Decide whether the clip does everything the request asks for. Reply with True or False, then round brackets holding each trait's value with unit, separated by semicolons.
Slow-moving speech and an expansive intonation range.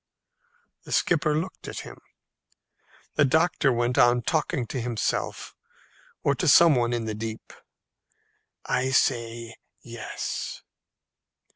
False (115 wpm; 4.2 semitones)